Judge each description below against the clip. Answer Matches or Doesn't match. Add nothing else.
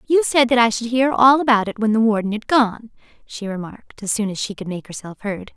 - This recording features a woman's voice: Matches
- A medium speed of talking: Doesn't match